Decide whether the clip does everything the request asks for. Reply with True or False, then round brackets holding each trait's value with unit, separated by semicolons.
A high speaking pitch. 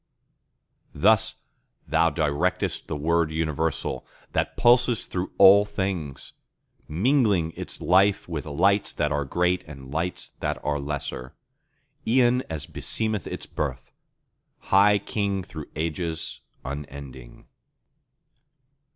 False (85 Hz)